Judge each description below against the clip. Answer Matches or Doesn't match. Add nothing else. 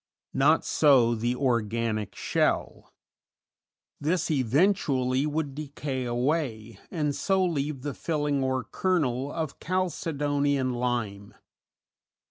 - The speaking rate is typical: Doesn't match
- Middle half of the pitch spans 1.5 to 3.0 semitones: Doesn't match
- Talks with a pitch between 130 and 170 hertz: Matches